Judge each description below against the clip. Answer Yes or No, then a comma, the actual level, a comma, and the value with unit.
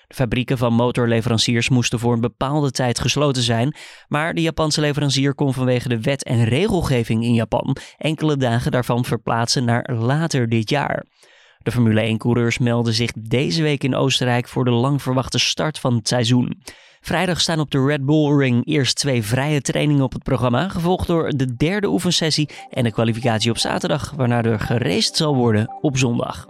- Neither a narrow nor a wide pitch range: Yes, average, 3.8 semitones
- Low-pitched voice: Yes, low, 130 Hz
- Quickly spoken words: No, average, 180 wpm